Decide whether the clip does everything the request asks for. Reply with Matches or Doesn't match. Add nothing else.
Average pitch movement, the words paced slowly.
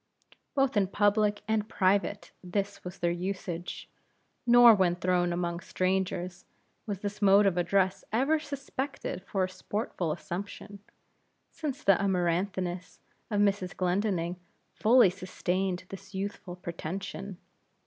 Doesn't match